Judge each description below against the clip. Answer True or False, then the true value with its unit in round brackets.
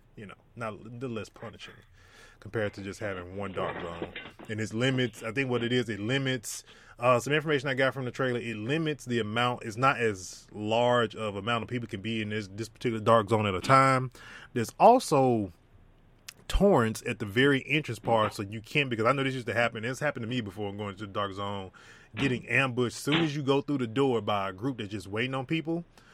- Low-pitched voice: True (120 Hz)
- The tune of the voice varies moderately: True (3.6 semitones)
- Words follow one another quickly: True (230 wpm)